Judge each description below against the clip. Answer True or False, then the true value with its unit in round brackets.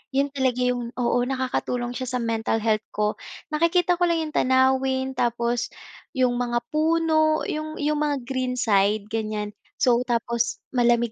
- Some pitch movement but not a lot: True (3.3 semitones)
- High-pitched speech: True (250 Hz)